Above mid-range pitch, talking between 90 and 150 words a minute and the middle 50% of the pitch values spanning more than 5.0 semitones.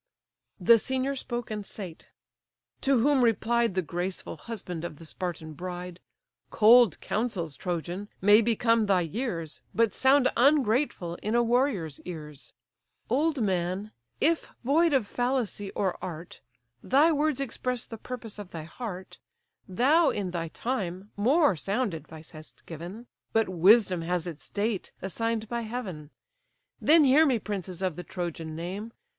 Yes: high, 210 Hz; average, 145 wpm; wide, 5.6 semitones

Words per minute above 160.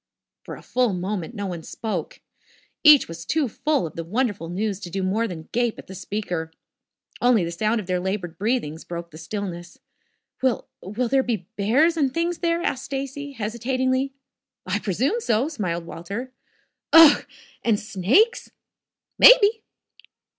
No: average, 155 wpm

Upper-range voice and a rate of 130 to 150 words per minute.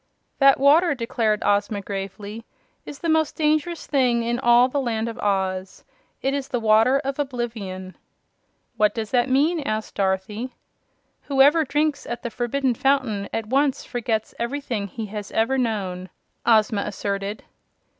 Yes: high, 235 Hz; average, 145 wpm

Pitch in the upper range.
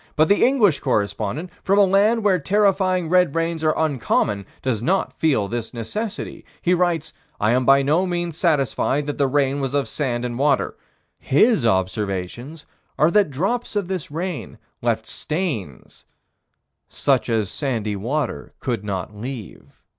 No: medium, 145 Hz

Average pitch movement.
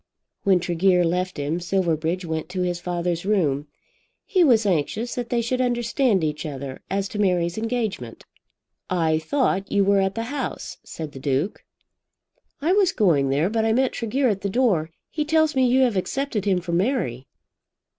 No: wide, 6.2 semitones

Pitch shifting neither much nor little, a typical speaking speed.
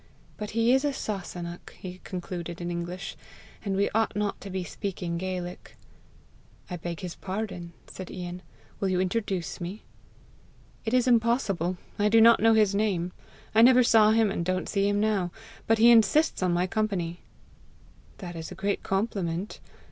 Yes: average, 3.5 semitones; average, 170 wpm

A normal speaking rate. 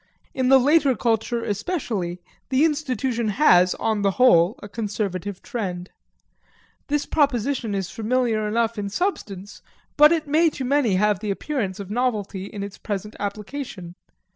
Yes: average, 145 wpm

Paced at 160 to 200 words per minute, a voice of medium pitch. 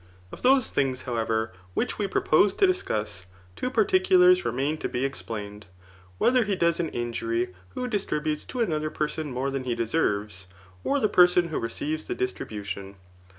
Yes: average, 170 wpm; medium, 150 Hz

